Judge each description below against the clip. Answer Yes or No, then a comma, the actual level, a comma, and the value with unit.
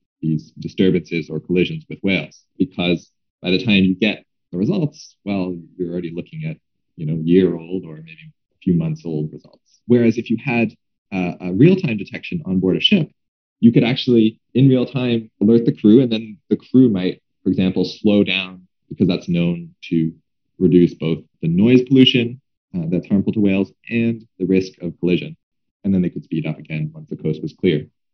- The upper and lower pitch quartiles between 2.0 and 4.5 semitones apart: No, wide, 5.5 semitones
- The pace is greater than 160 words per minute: Yes, average, 195 wpm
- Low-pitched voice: Yes, very low, 95 Hz